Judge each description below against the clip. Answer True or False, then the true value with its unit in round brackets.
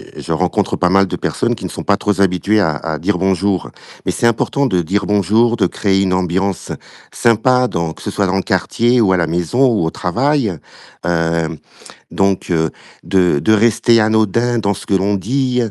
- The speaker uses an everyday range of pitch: True (4.1 semitones)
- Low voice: True (100 Hz)